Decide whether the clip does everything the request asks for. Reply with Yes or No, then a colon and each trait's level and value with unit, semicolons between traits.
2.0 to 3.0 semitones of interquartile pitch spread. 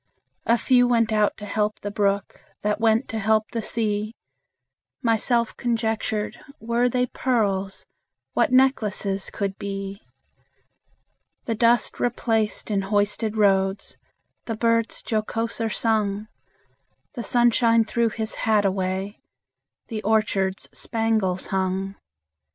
Yes: narrow, 2.4 semitones